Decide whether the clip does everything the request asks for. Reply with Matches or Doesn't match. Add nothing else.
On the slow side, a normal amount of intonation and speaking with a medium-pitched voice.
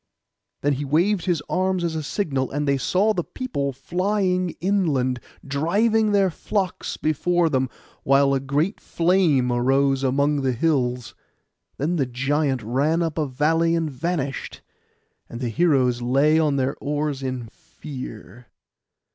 Doesn't match